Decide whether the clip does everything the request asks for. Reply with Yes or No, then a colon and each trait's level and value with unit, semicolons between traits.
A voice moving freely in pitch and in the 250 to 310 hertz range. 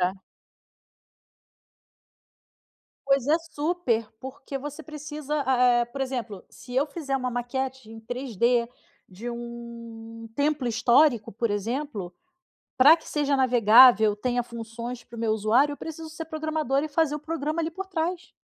No: average, 4.3 semitones; very high, 260 Hz